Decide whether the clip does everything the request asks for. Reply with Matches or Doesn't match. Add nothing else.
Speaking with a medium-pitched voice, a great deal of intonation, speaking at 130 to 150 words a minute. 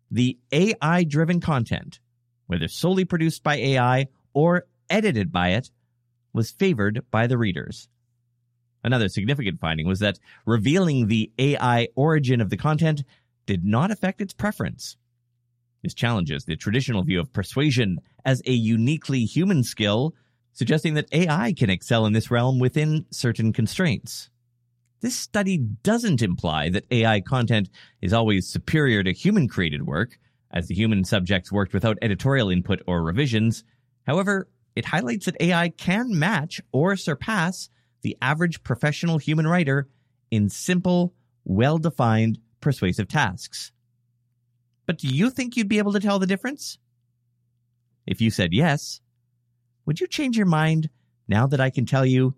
Doesn't match